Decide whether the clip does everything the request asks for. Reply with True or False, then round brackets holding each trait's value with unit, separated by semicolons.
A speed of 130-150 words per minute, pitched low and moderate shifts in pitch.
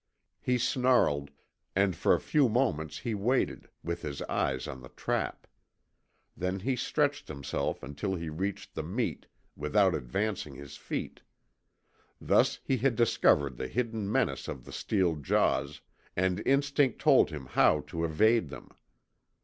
False (145 wpm; 95 Hz; 8.4 semitones)